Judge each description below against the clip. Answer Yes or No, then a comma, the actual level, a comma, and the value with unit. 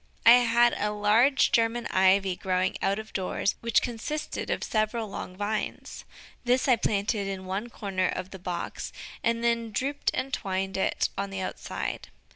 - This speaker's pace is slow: No, average, 165 wpm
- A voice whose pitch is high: Yes, high, 210 Hz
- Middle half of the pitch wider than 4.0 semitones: No, average, 3.5 semitones